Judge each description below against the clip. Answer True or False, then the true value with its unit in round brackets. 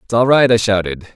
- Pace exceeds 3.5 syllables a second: True (5.7 syllables/s)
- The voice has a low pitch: True (110 Hz)